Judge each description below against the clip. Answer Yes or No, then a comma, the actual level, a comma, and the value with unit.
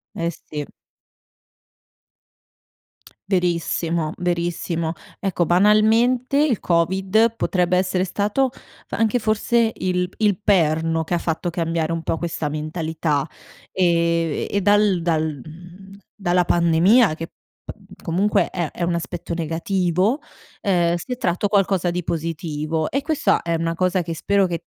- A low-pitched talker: No, medium, 175 Hz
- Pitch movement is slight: No, average, 3.1 semitones